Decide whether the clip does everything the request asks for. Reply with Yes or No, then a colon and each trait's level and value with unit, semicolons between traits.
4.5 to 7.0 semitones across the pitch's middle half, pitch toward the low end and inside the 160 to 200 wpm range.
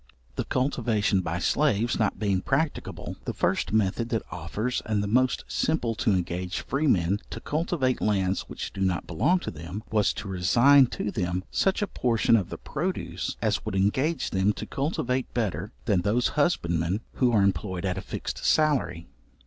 Yes: wide, 5.5 semitones; low, 105 Hz; average, 175 wpm